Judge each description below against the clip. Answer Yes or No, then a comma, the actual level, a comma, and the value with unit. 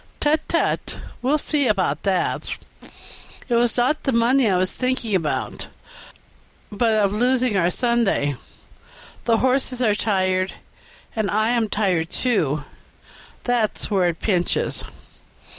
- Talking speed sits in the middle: No, slow, 125 wpm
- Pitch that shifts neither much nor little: Yes, average, 4.8 semitones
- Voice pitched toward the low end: No, high, 220 Hz